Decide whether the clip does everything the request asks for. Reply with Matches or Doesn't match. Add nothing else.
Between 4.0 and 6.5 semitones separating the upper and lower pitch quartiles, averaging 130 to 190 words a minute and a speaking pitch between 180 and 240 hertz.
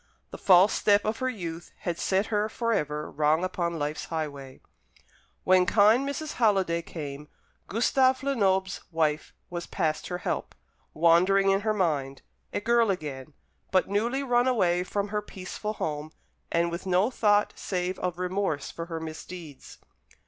Matches